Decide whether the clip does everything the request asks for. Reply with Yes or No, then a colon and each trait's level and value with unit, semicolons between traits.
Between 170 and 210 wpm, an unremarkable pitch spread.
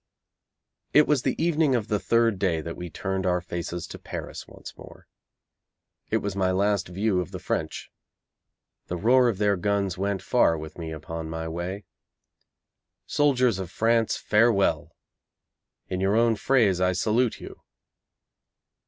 No: average, 155 wpm; average, 4.5 semitones